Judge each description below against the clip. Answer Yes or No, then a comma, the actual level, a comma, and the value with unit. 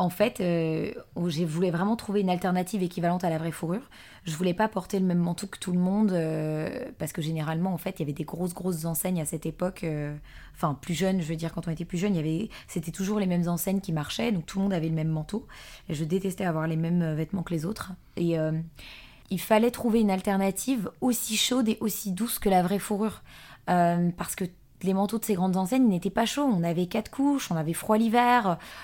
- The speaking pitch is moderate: Yes, medium, 180 Hz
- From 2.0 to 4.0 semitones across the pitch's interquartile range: Yes, average, 3.5 semitones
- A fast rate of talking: Yes, fast, 245 wpm